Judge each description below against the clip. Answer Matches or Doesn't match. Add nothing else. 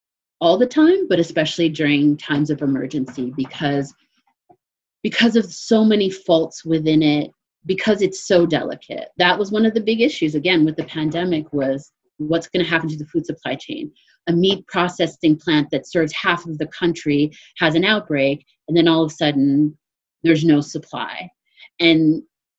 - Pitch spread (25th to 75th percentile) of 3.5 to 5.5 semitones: Matches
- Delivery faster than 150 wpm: Matches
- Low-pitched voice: Doesn't match